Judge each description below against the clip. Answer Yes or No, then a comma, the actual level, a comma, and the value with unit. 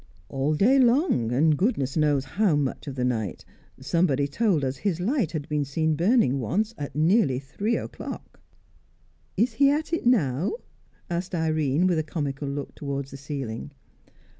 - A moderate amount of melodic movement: No, wide, 6.3 semitones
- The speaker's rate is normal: Yes, average, 165 wpm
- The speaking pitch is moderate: Yes, medium, 155 Hz